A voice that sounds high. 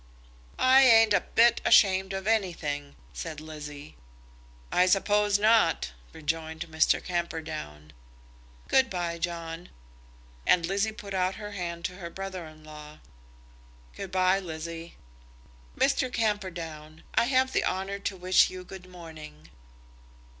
No: medium, 180 Hz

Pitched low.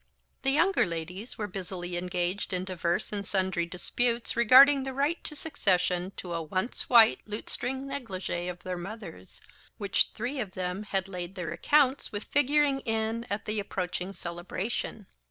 No: high, 200 Hz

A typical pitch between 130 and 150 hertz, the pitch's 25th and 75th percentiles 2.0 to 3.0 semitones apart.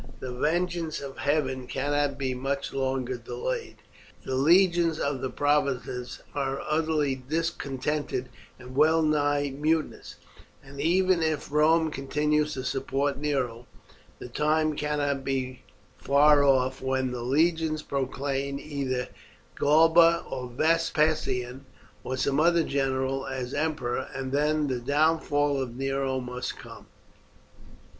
Yes: medium, 140 Hz; average, 2.7 semitones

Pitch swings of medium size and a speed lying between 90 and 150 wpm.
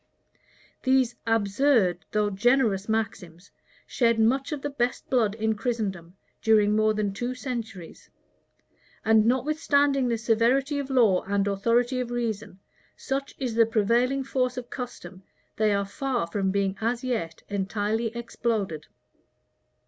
Yes: average, 3.8 semitones; slow, 135 wpm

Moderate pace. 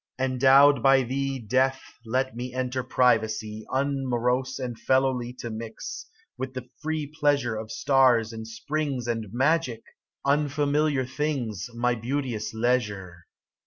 No: slow, 125 wpm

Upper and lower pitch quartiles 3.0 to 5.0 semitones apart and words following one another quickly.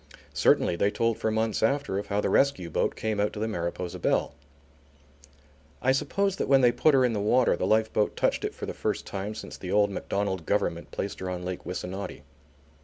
Yes: average, 3.5 semitones; fast, 210 wpm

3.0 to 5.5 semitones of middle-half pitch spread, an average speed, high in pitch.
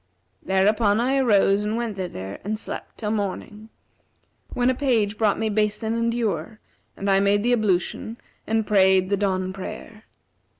No: narrow, 2.4 semitones; average, 160 wpm; high, 210 Hz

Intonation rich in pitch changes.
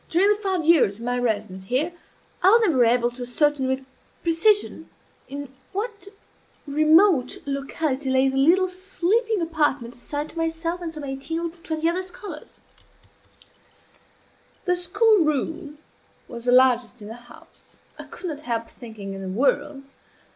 Yes: wide, 5.8 semitones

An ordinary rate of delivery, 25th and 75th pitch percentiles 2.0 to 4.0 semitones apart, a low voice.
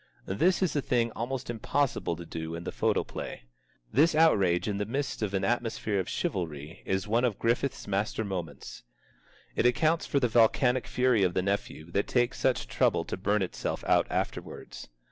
No: average, 180 wpm; average, 5.0 semitones; low, 110 Hz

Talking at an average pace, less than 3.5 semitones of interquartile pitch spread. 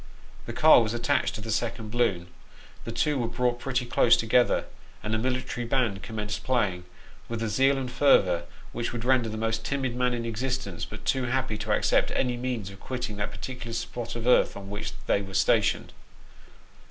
Yes: average, 190 wpm; average, 2.9 semitones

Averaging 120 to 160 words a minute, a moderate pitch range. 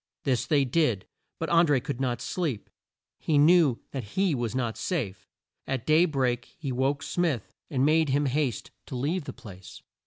No: average, 180 wpm; average, 4.3 semitones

